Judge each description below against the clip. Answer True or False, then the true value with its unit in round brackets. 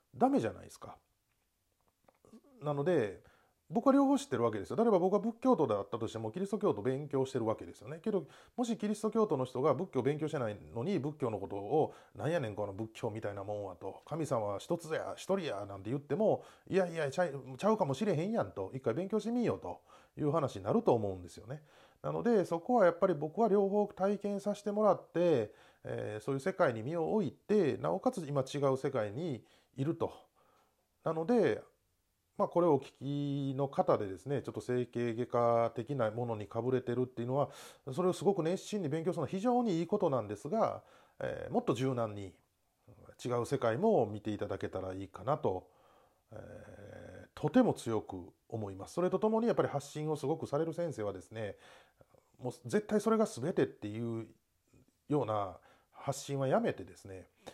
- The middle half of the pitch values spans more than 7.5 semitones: True (9.0 semitones)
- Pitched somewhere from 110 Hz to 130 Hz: False (140 Hz)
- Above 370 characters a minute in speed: True (385 characters per minute)